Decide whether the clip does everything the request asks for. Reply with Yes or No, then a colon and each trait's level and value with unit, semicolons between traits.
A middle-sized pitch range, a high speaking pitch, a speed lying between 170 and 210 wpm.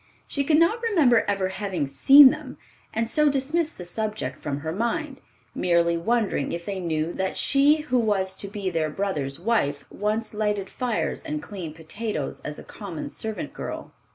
No: wide, 7.5 semitones; high, 210 Hz; average, 175 wpm